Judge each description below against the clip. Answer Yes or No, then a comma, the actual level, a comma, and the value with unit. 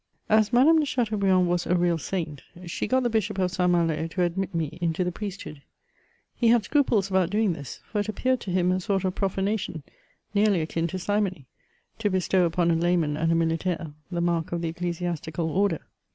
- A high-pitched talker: No, medium, 180 Hz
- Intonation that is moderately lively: Yes, average, 3.3 semitones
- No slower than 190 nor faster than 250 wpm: Yes, fast, 205 wpm